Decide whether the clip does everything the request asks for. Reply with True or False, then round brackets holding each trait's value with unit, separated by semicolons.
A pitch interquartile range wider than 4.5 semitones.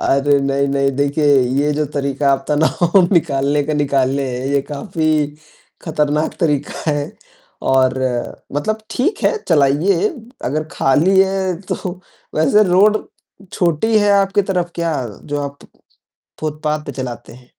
False (3.8 semitones)